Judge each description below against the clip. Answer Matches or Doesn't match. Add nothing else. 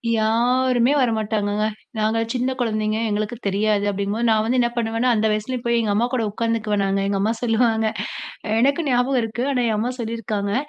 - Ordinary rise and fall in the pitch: Doesn't match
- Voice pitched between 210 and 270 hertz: Matches